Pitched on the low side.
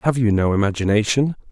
Yes: low, 115 Hz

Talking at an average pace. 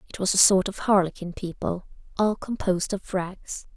Yes: average, 175 wpm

